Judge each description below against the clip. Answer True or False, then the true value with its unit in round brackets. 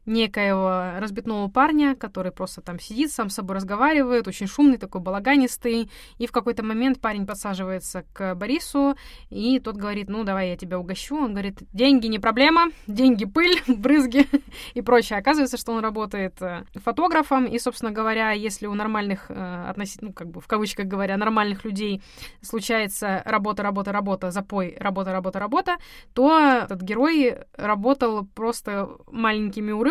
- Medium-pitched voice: False (220 Hz)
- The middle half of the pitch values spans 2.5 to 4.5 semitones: True (4.2 semitones)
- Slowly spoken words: False (150 wpm)